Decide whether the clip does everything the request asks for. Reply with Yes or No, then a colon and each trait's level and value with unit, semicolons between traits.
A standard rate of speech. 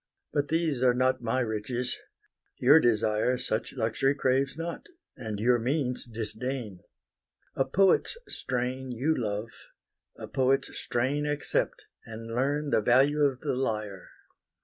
No: slow, 130 wpm